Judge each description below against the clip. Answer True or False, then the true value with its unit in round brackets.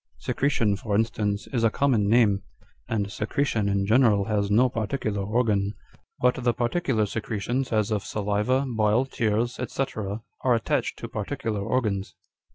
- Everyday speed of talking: True (150 wpm)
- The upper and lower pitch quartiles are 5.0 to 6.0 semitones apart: False (2.9 semitones)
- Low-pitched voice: True (110 Hz)